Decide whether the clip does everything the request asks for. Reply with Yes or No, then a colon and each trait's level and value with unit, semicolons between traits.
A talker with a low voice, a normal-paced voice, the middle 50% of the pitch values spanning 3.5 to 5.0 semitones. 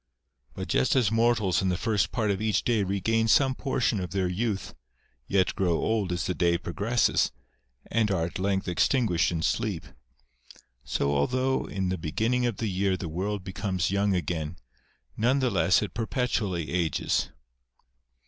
Yes: low, 100 Hz; average, 165 wpm; average, 4.1 semitones